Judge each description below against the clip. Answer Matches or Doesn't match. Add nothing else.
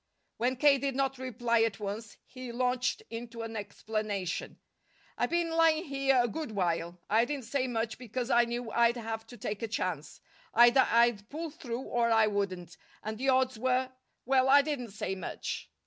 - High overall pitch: Matches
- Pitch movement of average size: Matches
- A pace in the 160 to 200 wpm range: Matches